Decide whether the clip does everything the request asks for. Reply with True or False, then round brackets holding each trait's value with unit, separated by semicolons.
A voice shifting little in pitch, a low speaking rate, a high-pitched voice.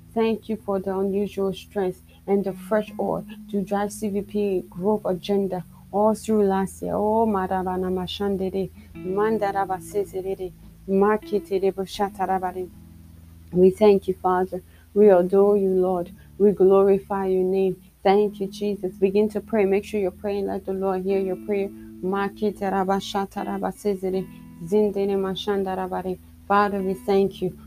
True (1.5 semitones; 115 wpm; 195 Hz)